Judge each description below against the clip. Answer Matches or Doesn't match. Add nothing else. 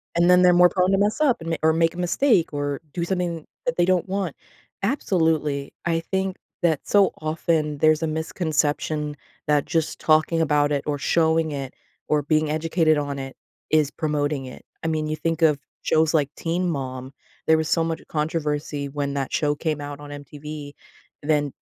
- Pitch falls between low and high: Matches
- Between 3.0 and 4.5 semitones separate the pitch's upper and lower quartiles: Doesn't match